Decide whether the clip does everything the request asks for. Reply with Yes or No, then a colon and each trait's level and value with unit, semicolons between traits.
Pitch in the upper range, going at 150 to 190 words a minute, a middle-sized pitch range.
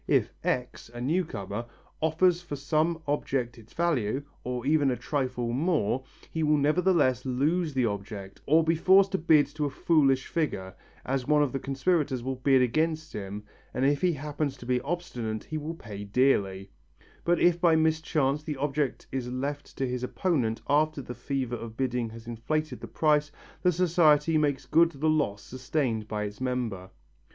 No: medium, 140 Hz; average, 180 wpm; average, 4.2 semitones